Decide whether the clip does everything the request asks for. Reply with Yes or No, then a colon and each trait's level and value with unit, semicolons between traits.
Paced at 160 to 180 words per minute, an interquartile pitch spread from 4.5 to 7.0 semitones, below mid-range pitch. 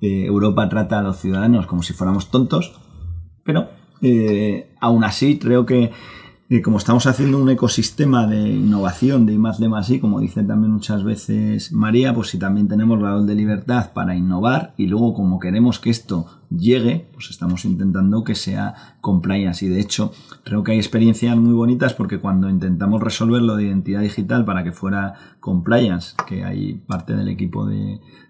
No: average, 175 wpm; average, 3.4 semitones; low, 105 Hz